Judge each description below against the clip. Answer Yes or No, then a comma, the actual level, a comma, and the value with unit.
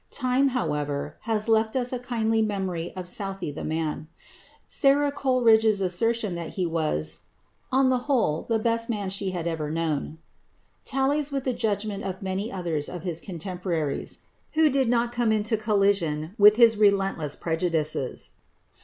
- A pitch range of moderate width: No, wide, 5.7 semitones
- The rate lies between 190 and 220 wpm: No, average, 155 wpm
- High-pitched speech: Yes, high, 200 Hz